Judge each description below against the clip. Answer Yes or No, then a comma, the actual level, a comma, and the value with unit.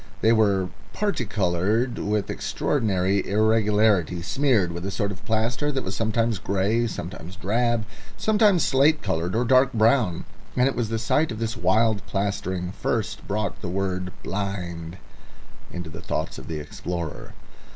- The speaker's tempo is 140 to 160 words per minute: Yes, average, 150 wpm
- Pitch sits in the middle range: No, low, 105 Hz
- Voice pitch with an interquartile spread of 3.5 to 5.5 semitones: Yes, average, 4.0 semitones